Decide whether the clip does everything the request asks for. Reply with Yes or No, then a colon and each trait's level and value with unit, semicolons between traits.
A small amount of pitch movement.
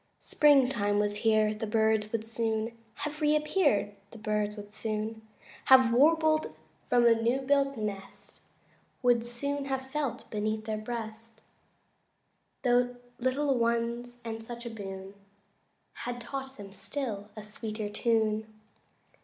No: average, 3.4 semitones